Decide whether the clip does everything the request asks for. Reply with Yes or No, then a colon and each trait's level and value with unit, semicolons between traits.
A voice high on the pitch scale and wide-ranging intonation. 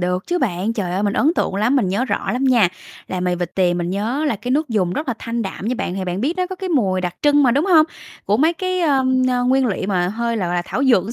Yes: high, 230 Hz; wide, 6.8 semitones